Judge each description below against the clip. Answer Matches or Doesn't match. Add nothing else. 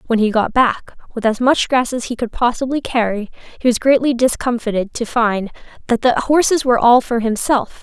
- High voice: Matches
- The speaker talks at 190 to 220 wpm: Matches